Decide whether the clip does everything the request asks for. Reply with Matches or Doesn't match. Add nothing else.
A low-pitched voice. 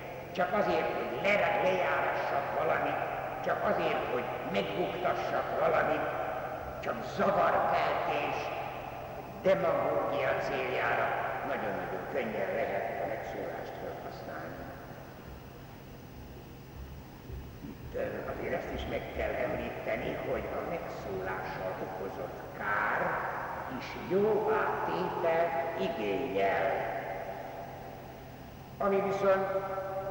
Matches